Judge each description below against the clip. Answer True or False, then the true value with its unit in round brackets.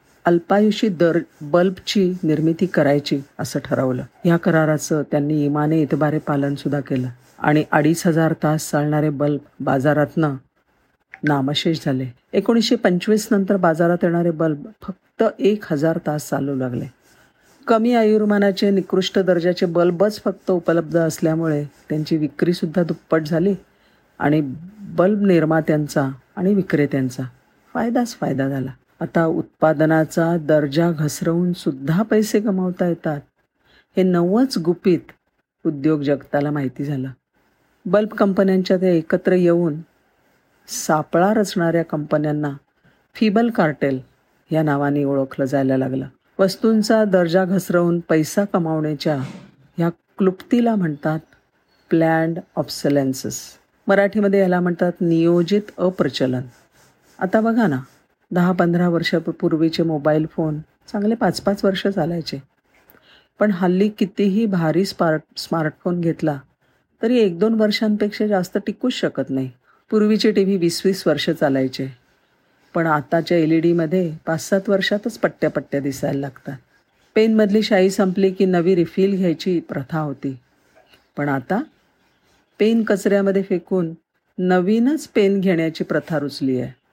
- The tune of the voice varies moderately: True (4.5 semitones)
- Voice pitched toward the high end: False (170 Hz)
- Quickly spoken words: False (115 wpm)